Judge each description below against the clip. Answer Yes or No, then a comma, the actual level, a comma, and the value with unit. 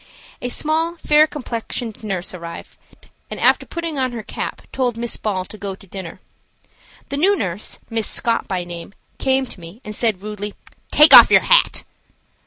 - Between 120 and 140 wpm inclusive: No, average, 175 wpm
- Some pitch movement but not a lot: No, wide, 5.7 semitones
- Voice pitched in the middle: No, high, 225 Hz